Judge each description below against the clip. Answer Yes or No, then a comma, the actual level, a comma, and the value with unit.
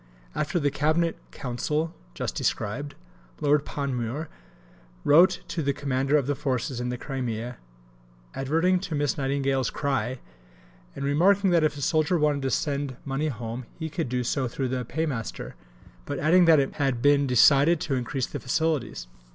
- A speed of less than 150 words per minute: No, average, 160 wpm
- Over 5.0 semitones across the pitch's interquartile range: No, average, 3.3 semitones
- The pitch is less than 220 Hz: Yes, medium, 140 Hz